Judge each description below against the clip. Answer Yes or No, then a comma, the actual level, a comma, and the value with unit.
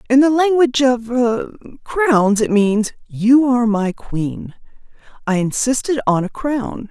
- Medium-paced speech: No, slow, 130 wpm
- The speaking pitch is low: No, high, 240 Hz